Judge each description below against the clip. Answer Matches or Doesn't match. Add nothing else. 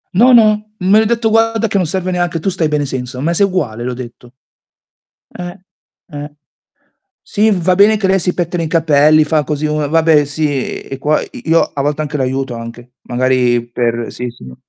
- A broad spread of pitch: Matches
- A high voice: Doesn't match